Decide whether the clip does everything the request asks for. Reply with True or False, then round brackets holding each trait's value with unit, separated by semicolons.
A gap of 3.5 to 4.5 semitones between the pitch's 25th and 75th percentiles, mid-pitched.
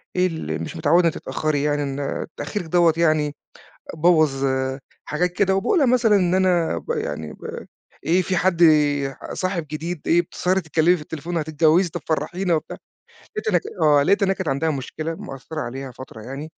True (3.8 semitones; 165 Hz)